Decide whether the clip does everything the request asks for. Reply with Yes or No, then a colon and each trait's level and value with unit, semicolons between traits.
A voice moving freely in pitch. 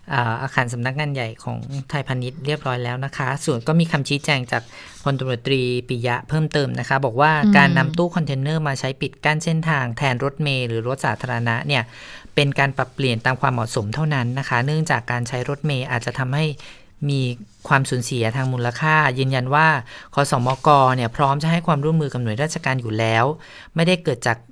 No: average, 3.2 semitones